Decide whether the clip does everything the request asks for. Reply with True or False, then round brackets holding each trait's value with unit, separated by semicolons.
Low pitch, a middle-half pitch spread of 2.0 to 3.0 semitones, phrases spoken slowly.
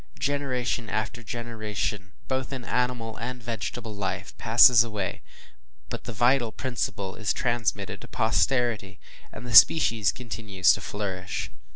True (115 Hz; 2.7 semitones; 130 wpm)